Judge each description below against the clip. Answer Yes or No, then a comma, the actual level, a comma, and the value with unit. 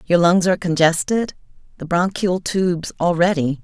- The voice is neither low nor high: Yes, medium, 175 Hz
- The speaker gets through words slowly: Yes, slow, 130 wpm